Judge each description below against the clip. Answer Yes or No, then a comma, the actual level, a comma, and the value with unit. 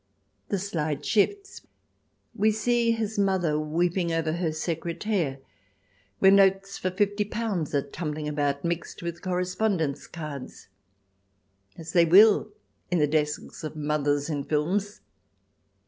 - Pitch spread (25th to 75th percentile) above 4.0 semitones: Yes, average, 4.7 semitones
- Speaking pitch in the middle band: Yes, medium, 170 Hz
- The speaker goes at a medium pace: No, slow, 125 wpm